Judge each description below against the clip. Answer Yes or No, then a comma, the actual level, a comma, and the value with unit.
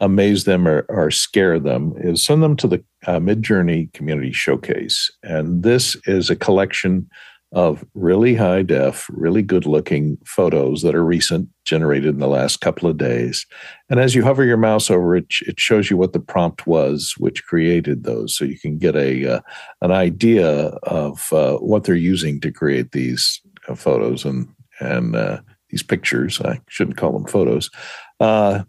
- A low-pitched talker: Yes, very low, 90 Hz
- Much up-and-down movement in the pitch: Yes, wide, 6.1 semitones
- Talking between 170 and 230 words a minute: Yes, average, 180 wpm